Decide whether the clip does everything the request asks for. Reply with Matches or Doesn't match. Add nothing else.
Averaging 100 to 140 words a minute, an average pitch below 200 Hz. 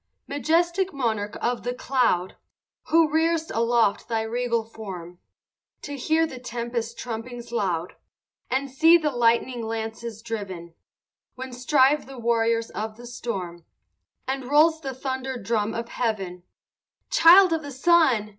Doesn't match